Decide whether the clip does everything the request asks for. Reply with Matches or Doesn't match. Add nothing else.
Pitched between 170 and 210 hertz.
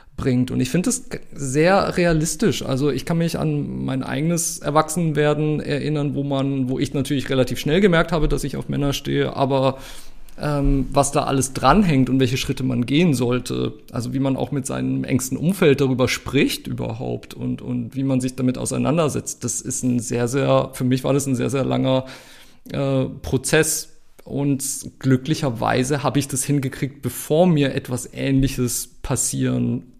Doesn't match